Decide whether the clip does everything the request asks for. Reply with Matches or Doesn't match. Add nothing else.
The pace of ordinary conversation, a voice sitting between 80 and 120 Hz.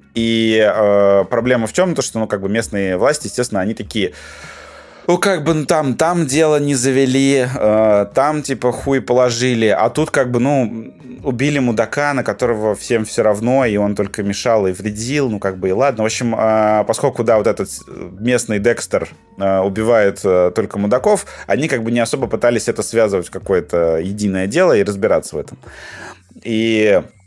Doesn't match